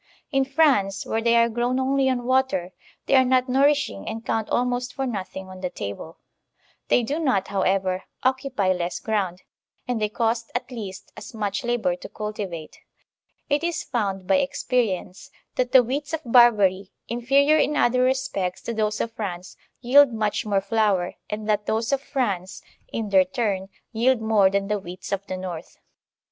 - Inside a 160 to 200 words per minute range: Yes, average, 175 wpm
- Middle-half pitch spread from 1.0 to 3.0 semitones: No, average, 4.9 semitones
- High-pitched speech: Yes, high, 225 Hz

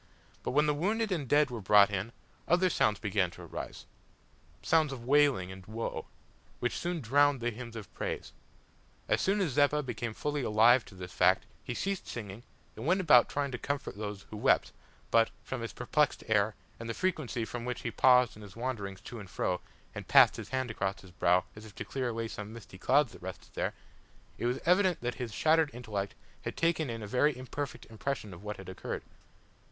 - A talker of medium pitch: No, low, 120 Hz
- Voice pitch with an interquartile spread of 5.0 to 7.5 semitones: Yes, wide, 5.4 semitones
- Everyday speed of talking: No, fast, 210 wpm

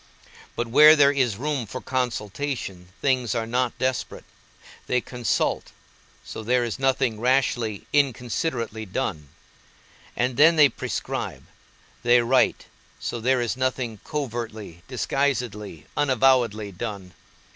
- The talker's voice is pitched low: Yes, low, 125 Hz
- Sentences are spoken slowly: Yes, slow, 115 wpm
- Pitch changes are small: No, average, 3.2 semitones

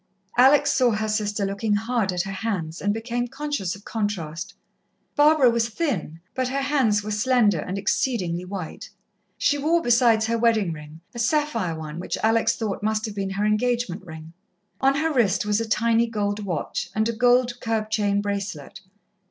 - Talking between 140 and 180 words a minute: Yes, average, 175 wpm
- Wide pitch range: No, average, 3.7 semitones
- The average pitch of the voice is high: Yes, high, 215 Hz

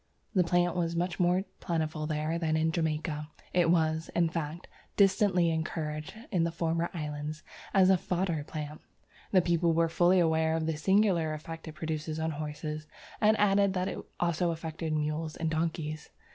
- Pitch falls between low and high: Yes, medium, 165 Hz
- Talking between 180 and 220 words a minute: No, average, 170 wpm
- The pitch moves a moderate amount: No, narrow, 2.1 semitones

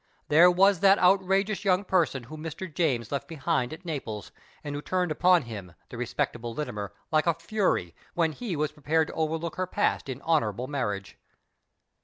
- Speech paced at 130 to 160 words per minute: No, average, 175 wpm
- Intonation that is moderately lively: No, wide, 5.9 semitones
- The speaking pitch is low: No, medium, 155 Hz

